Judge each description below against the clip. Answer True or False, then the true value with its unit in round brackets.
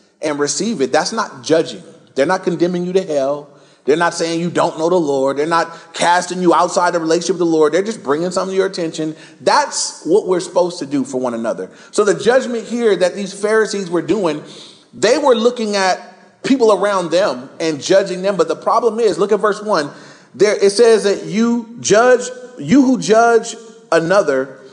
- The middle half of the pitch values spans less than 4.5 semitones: False (4.8 semitones)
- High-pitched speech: False (180 Hz)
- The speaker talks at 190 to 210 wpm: True (200 wpm)